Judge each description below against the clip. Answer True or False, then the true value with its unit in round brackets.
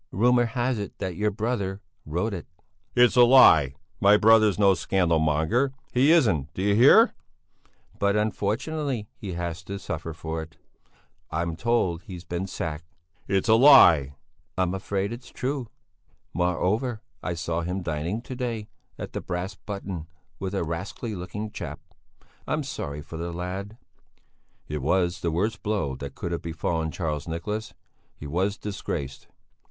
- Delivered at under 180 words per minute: True (150 wpm)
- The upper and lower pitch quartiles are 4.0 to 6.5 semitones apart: True (4.7 semitones)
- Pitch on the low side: True (95 Hz)